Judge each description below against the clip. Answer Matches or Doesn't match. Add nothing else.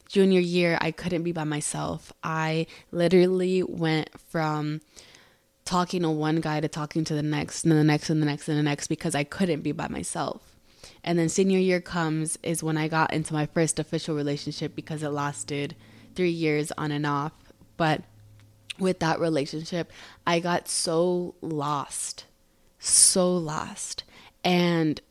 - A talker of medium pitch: Matches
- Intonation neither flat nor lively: Doesn't match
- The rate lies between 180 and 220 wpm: Doesn't match